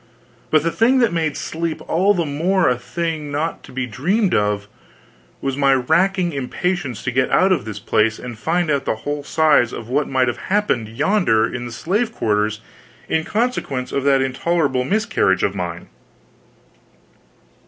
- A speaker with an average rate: Yes, average, 170 wpm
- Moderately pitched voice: Yes, medium, 145 Hz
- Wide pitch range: Yes, wide, 6.3 semitones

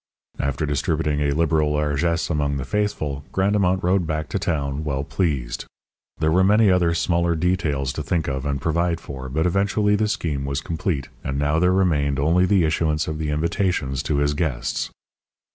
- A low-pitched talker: Yes, very low, 80 Hz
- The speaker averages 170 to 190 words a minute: Yes, average, 180 wpm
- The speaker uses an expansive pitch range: No, average, 3.8 semitones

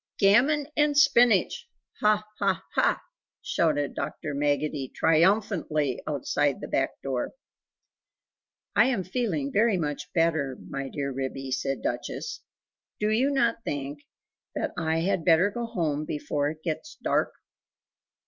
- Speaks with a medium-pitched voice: Yes, medium, 165 Hz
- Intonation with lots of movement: Yes, wide, 6.9 semitones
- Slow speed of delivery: Yes, slow, 130 wpm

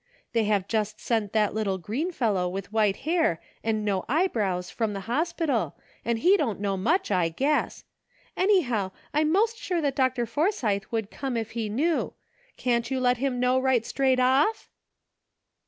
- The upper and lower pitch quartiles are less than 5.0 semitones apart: No, wide, 5.6 semitones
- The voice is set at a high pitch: Yes, high, 235 Hz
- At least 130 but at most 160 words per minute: No, average, 170 wpm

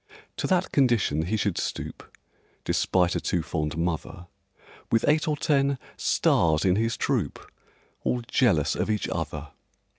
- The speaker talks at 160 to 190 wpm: No, average, 145 wpm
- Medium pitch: No, low, 105 Hz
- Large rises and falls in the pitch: Yes, wide, 7.7 semitones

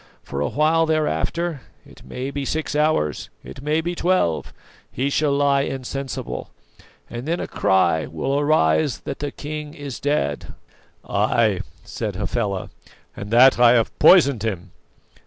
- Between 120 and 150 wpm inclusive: Yes, average, 145 wpm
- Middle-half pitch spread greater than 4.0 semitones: Yes, wide, 5.5 semitones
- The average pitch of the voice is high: No, medium, 140 Hz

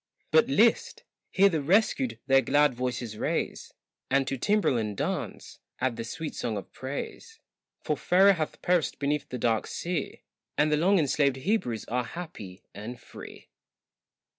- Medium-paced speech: Yes, average, 155 wpm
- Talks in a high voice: No, medium, 140 Hz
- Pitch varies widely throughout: Yes, wide, 6.5 semitones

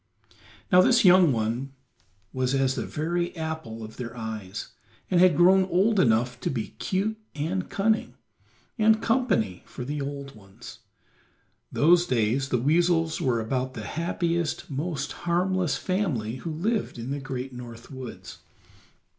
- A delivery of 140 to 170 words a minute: Yes, average, 145 wpm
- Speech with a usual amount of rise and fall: No, wide, 6.3 semitones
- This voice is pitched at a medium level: Yes, medium, 145 Hz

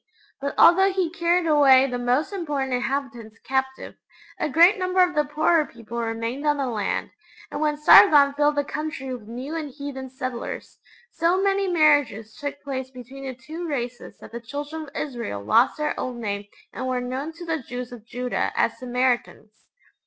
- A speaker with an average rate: Yes, average, 180 wpm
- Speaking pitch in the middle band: No, very high, 275 Hz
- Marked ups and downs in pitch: No, average, 3.8 semitones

